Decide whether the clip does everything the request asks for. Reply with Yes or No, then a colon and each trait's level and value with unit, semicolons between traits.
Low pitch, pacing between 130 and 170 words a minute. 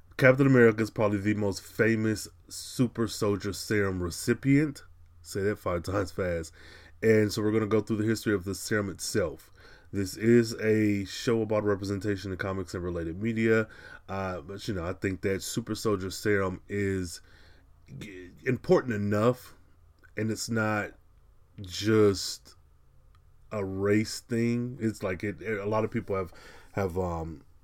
Yes: low, 100 Hz; average, 150 wpm